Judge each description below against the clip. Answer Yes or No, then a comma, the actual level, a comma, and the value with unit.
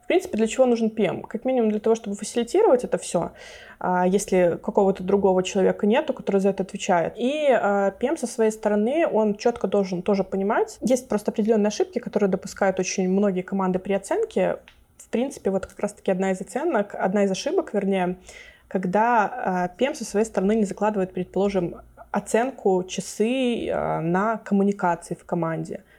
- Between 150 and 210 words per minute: Yes, fast, 160 wpm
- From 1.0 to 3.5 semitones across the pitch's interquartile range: Yes, average, 2.9 semitones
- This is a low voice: No, high, 205 Hz